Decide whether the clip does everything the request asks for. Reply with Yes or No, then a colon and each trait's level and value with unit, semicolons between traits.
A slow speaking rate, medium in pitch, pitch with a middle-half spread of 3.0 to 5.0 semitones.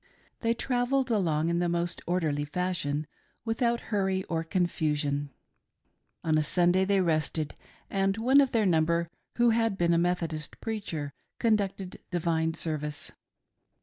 Yes: slow, 130 wpm; medium, 175 Hz; average, 4.5 semitones